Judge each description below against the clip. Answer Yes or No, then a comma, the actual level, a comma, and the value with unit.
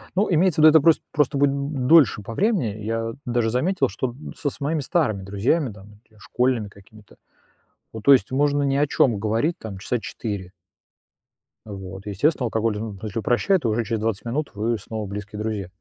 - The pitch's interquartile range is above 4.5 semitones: Yes, average, 5.3 semitones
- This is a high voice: No, low, 115 Hz